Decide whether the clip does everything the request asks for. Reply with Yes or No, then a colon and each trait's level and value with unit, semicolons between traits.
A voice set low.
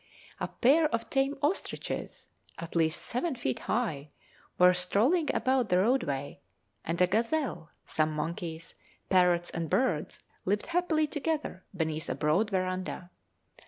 No: medium, 185 Hz